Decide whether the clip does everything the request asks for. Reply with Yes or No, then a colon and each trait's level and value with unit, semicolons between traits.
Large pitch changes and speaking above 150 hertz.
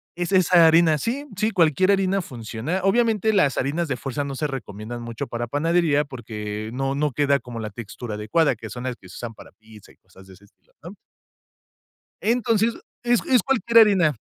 No: wide, 8.3 semitones; medium, 145 Hz